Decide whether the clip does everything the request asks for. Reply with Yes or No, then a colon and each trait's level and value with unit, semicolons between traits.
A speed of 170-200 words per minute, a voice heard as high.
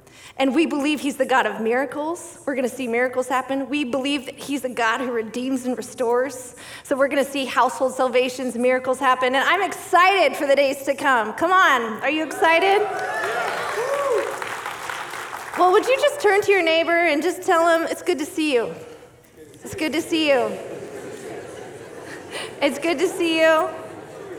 Yes: average, 180 wpm; very high, 290 Hz